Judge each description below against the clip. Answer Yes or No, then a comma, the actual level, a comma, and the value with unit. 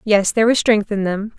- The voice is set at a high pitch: Yes, high, 210 Hz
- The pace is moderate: No, fast, 260 wpm